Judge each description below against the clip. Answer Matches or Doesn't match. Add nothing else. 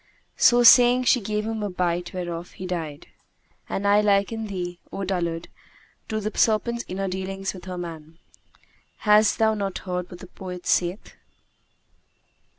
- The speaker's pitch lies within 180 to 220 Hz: Matches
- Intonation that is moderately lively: Matches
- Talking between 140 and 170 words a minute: Matches